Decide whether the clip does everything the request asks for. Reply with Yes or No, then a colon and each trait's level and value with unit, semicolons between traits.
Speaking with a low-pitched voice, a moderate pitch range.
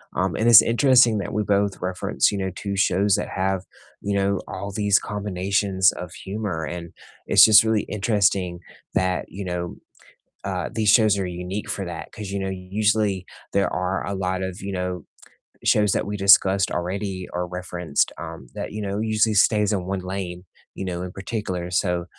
No: very low, 95 Hz; narrow, 2.2 semitones